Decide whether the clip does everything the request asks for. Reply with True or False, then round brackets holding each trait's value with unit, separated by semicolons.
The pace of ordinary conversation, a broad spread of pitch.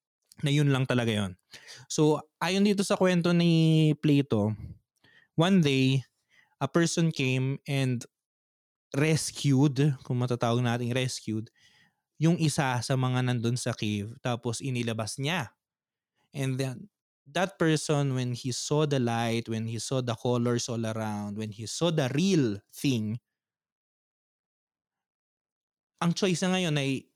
False (135 wpm; 4.8 semitones)